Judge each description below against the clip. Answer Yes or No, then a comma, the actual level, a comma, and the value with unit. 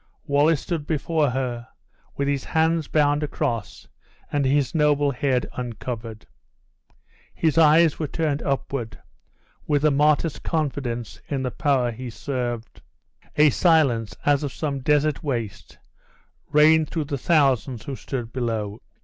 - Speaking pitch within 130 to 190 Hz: Yes, medium, 140 Hz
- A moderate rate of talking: No, slow, 130 wpm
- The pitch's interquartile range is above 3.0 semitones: Yes, average, 3.5 semitones